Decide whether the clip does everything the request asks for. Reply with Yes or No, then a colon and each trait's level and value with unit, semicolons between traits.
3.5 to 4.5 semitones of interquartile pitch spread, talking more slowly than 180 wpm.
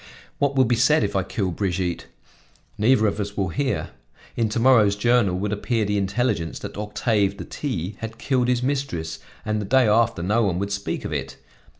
No: average, 3.8 semitones; average, 200 wpm